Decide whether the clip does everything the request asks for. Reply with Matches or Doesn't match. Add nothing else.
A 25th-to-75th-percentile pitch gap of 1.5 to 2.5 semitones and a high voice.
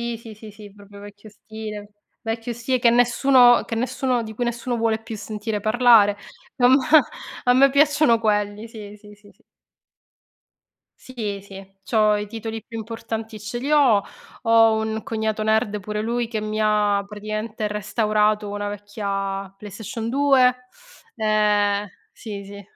Matches